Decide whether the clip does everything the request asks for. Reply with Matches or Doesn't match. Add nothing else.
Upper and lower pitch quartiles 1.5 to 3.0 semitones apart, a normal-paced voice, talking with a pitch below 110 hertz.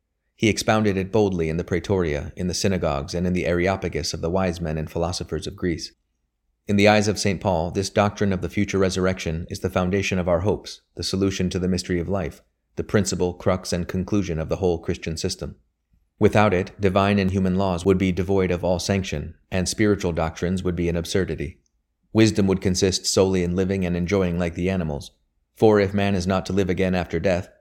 Doesn't match